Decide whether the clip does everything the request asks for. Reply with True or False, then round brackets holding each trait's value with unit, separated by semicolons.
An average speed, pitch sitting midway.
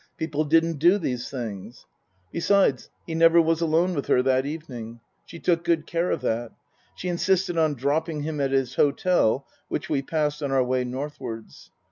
True (175 wpm; 150 Hz)